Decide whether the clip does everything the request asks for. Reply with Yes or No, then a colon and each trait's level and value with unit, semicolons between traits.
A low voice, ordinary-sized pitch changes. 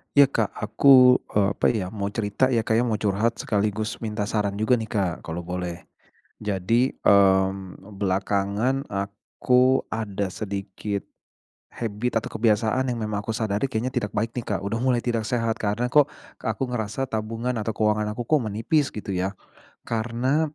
Yes: low, 110 Hz; average, 3.1 semitones